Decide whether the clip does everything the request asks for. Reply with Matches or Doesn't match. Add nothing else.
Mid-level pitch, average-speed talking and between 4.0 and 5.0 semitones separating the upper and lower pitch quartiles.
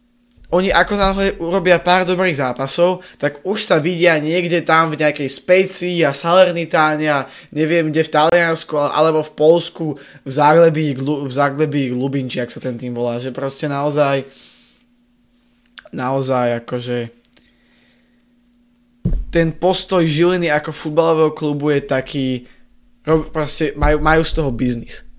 Matches